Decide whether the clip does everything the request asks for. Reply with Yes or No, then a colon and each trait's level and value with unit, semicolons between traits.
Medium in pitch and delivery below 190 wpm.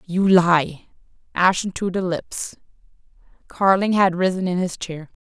Yes: medium, 180 Hz; average, 140 wpm